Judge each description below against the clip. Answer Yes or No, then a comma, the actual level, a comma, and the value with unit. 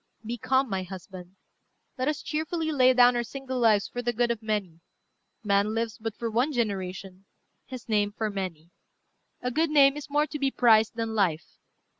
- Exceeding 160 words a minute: Yes, average, 185 wpm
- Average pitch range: Yes, average, 4.5 semitones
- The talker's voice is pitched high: Yes, high, 230 Hz